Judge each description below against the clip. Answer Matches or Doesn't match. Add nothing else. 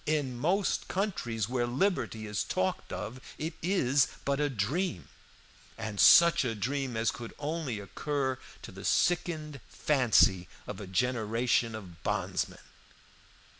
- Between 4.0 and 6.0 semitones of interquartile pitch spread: Matches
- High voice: Doesn't match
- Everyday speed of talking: Doesn't match